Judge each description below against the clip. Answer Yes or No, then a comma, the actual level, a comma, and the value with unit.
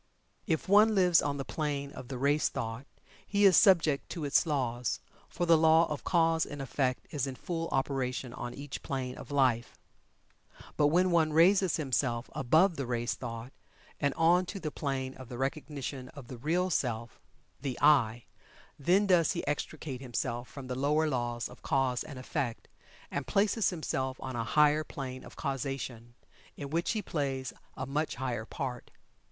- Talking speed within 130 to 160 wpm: No, average, 175 wpm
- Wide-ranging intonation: No, average, 4.0 semitones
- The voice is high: No, medium, 140 Hz